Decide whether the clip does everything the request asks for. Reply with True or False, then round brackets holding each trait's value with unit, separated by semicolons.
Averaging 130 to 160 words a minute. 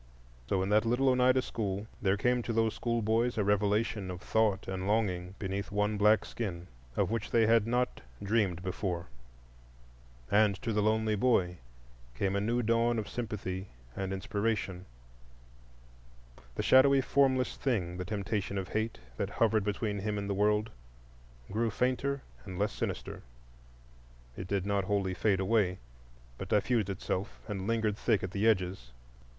True (150 wpm)